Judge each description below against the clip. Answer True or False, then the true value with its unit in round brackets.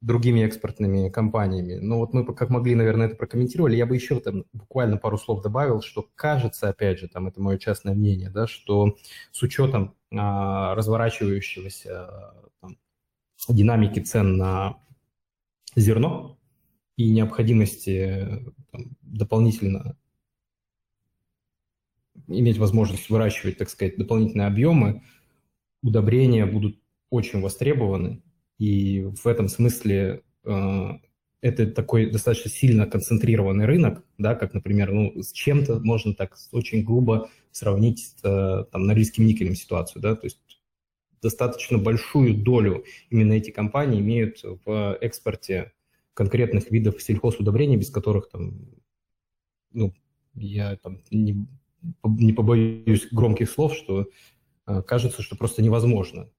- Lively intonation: False (2.8 semitones)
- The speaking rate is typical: True (120 wpm)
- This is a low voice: True (110 Hz)